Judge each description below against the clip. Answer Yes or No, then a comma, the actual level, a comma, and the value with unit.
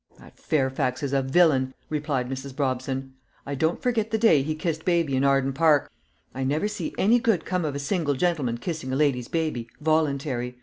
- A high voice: No, medium, 145 Hz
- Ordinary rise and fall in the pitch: Yes, average, 3.5 semitones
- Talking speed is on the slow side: No, average, 190 wpm